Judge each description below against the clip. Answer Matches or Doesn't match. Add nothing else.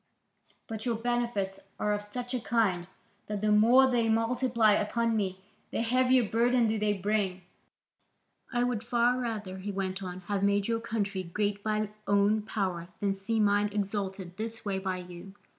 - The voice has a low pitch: Doesn't match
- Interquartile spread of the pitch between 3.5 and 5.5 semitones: Doesn't match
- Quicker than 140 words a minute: Matches